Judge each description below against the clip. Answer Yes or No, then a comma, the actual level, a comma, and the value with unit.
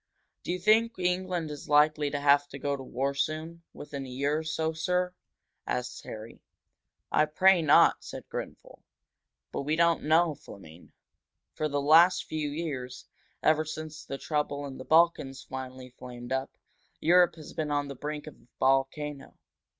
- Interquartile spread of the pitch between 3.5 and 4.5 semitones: No, average, 2.8 semitones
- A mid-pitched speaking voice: Yes, medium, 150 Hz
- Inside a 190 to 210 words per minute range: No, average, 165 wpm